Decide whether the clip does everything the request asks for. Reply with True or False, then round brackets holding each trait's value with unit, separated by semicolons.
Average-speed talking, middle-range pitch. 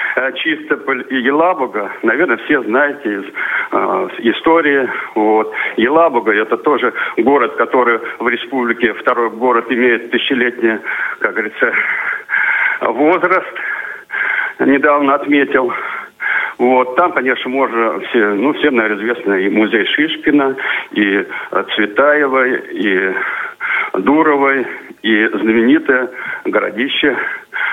False (95 wpm; 155 Hz)